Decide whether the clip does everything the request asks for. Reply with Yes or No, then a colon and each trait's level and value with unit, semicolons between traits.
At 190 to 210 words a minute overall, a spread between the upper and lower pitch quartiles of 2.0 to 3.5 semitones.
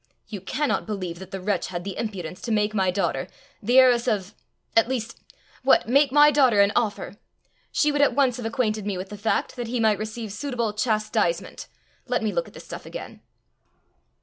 No: average, 200 wpm; average, 4.0 semitones